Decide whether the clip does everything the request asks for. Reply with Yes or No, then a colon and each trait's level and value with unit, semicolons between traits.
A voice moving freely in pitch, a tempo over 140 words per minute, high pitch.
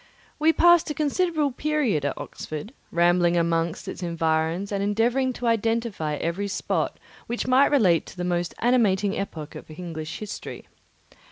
Yes: wide, 6.6 semitones; average, 150 wpm; high, 200 Hz